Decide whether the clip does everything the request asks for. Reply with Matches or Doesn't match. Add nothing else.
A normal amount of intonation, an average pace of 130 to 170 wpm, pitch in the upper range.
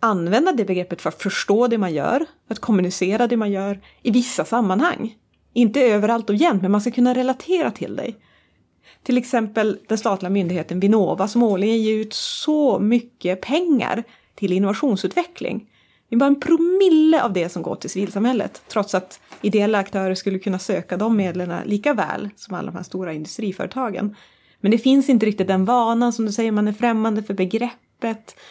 Doesn't match